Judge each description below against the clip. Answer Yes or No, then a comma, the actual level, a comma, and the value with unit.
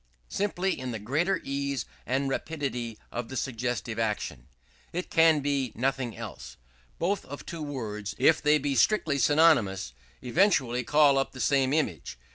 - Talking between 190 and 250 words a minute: No, average, 155 wpm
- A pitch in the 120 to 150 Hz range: Yes, low, 135 Hz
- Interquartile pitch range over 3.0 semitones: Yes, average, 4.2 semitones